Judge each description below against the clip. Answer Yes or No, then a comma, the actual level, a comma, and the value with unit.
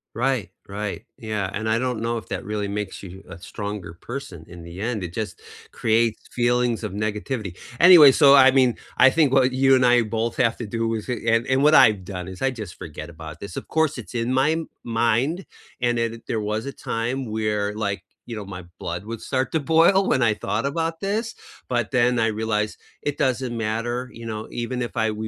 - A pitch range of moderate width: Yes, average, 3.6 semitones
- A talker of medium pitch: No, low, 115 Hz